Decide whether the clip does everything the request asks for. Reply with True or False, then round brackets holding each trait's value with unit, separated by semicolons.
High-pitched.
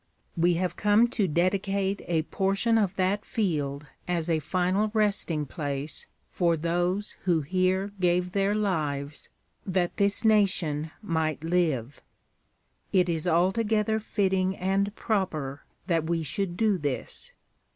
False (180 Hz)